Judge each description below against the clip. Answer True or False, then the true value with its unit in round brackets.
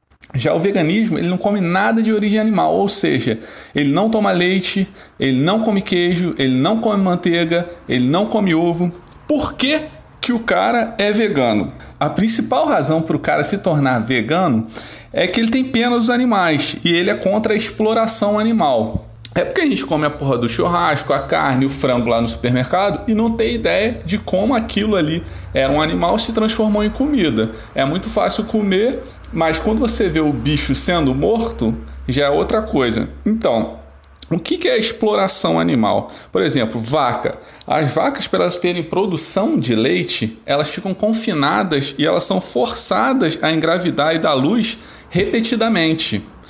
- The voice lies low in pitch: False (185 Hz)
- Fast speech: False (175 wpm)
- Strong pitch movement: True (7.1 semitones)